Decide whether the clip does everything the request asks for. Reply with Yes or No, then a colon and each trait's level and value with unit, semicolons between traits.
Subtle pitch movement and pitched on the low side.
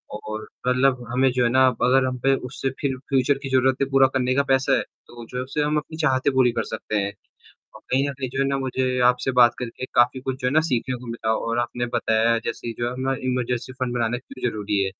Yes: narrow, 1.7 semitones; low, 130 Hz